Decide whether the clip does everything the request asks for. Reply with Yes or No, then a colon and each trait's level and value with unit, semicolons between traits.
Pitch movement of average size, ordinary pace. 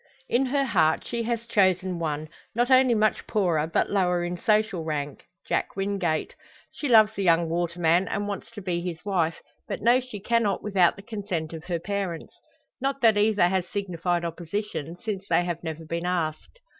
Yes: average, 4.0 semitones; average, 180 wpm